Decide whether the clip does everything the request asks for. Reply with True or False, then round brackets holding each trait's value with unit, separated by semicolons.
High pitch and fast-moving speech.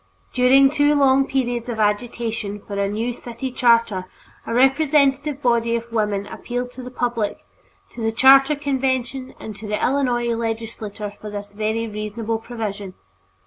False (235 Hz; 150 wpm)